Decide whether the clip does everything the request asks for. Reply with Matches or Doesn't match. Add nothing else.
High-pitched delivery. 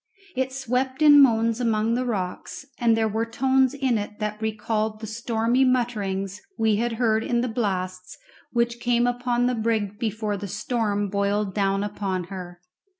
Matches